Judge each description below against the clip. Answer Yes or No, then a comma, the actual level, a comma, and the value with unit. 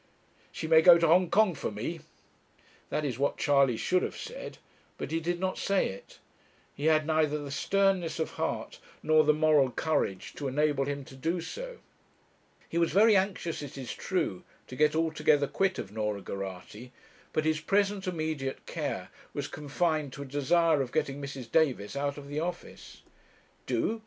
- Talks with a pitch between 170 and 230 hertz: No, medium, 155 Hz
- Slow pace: No, average, 175 wpm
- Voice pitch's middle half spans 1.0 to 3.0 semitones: No, average, 3.7 semitones